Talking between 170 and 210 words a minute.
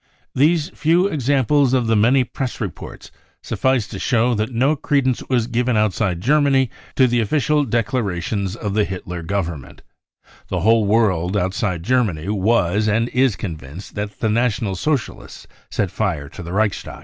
No: average, 160 wpm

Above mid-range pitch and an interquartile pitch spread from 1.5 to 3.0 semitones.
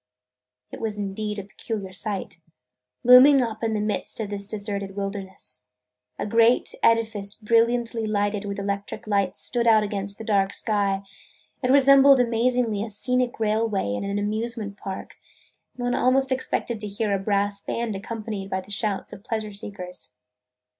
Yes: high, 210 Hz; narrow, 2.5 semitones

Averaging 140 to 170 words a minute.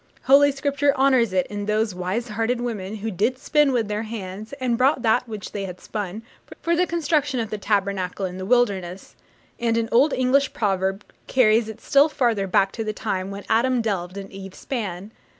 No: average, 195 wpm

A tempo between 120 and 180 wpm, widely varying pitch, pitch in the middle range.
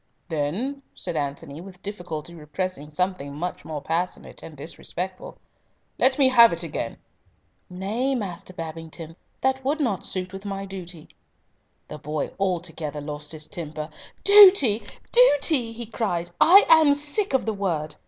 Yes: average, 145 wpm; wide, 6.9 semitones; medium, 180 Hz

